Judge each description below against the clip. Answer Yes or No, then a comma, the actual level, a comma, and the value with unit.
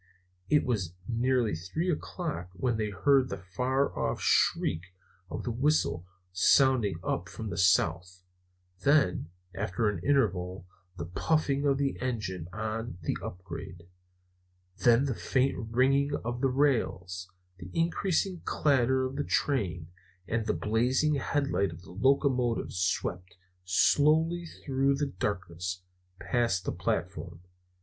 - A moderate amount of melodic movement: No, wide, 7.0 semitones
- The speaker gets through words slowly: Yes, slow, 130 wpm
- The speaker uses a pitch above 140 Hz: No, low, 115 Hz